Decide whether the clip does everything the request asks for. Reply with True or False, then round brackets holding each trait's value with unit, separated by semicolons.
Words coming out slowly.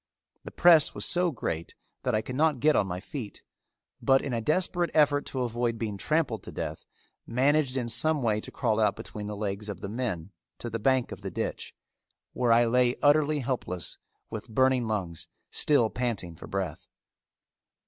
False (185 wpm)